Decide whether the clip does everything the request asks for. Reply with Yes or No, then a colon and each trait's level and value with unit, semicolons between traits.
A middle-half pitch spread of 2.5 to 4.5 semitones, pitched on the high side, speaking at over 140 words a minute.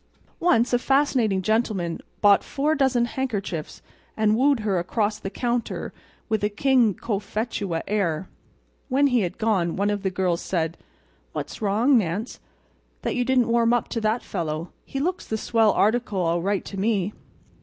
Yes: average, 4.1 semitones; high, 215 Hz; average, 165 wpm